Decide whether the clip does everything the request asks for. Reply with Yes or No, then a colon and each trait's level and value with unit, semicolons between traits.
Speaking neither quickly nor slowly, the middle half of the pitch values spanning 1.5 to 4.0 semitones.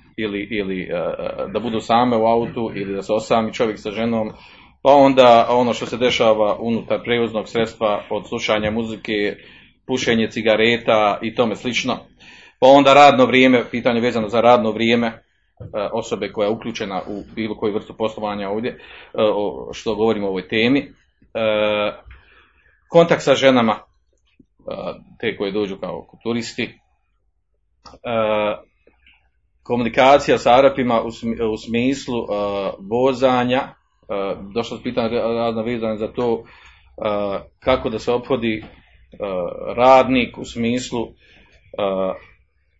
Yes: average, 135 wpm; narrow, 2.5 semitones